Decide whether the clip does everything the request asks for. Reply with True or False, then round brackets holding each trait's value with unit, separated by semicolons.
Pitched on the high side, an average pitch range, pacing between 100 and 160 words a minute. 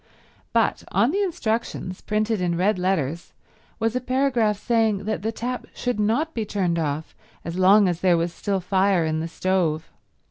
False (200 Hz; 4.5 semitones; 175 wpm)